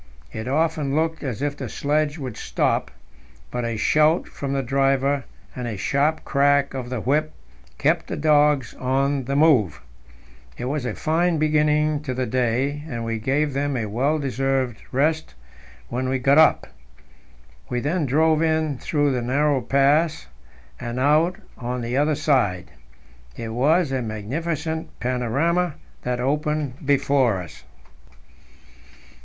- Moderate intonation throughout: Yes, average, 3.4 semitones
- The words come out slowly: No, average, 145 wpm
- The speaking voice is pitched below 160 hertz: Yes, medium, 140 Hz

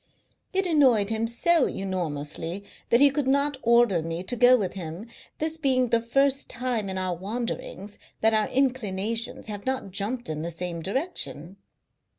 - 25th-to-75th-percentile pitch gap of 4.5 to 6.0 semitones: Yes, wide, 5.6 semitones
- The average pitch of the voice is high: Yes, high, 225 Hz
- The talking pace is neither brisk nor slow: Yes, average, 165 wpm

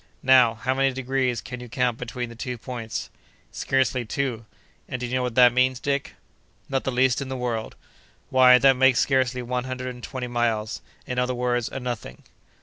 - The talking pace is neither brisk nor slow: Yes, average, 190 wpm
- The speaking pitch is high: No, low, 125 Hz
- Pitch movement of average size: No, narrow, 1.3 semitones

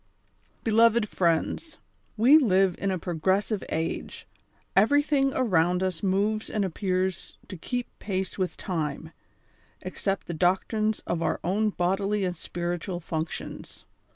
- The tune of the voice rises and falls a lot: No, average, 3.4 semitones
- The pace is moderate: No, slow, 125 wpm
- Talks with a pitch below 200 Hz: Yes, high, 190 Hz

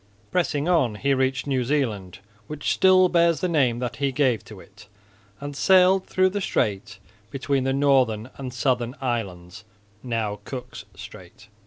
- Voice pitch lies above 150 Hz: No, low, 130 Hz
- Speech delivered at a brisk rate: No, average, 155 wpm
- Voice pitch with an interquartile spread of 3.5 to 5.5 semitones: Yes, average, 4.7 semitones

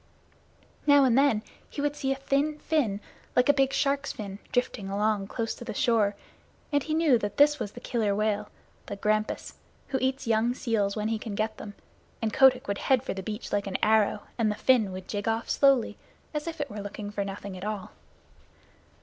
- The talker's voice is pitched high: Yes, high, 225 Hz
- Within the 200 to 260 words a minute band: Yes, fast, 205 wpm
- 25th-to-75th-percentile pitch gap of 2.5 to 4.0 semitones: No, average, 4.7 semitones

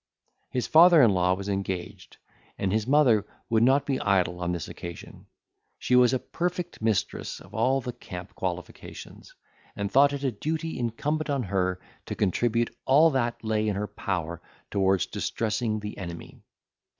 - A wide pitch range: Yes, wide, 5.8 semitones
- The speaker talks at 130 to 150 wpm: No, average, 160 wpm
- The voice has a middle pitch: No, low, 110 Hz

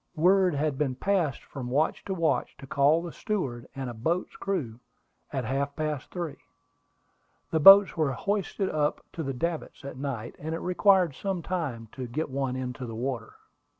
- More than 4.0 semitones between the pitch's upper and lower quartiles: Yes, average, 5.0 semitones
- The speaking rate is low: No, average, 180 wpm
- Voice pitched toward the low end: No, medium, 150 Hz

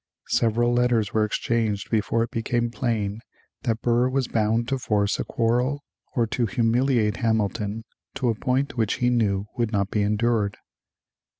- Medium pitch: No, low, 115 Hz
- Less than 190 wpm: Yes, average, 160 wpm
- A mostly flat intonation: Yes, narrow, 2.1 semitones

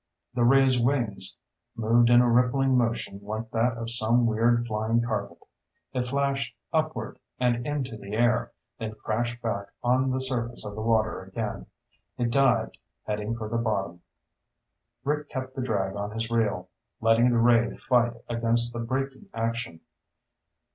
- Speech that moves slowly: No, average, 155 wpm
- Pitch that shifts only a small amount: Yes, narrow, 2.1 semitones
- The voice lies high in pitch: No, low, 115 Hz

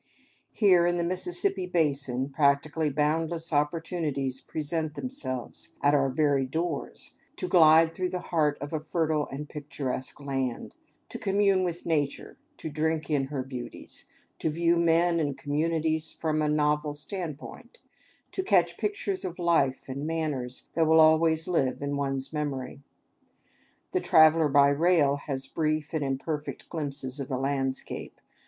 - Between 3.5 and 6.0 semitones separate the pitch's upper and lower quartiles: No, average, 2.9 semitones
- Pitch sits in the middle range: Yes, medium, 155 Hz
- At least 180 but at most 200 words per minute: No, average, 145 wpm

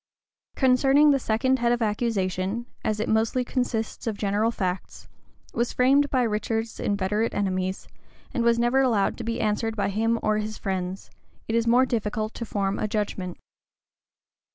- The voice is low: No, high, 220 Hz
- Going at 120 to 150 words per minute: No, average, 160 wpm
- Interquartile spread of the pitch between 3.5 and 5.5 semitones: No, average, 2.7 semitones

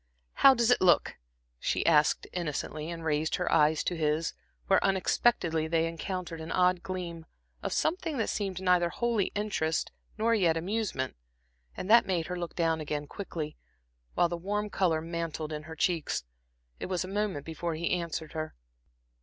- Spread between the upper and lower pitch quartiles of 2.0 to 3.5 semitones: Yes, average, 3.1 semitones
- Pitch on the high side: No, medium, 170 Hz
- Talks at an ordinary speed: Yes, average, 170 wpm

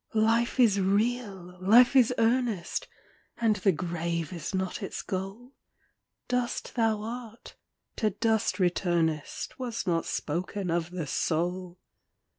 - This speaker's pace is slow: Yes, slow, 120 wpm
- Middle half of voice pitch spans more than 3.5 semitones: Yes, average, 4.6 semitones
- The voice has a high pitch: Yes, high, 195 Hz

